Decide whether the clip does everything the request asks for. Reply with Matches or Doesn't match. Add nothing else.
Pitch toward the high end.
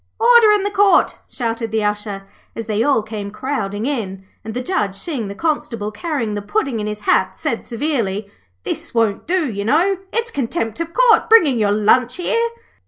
Matches